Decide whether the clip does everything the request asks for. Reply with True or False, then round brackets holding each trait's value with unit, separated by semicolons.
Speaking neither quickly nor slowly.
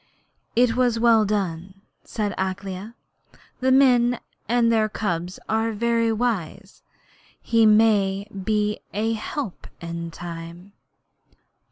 False (100 wpm)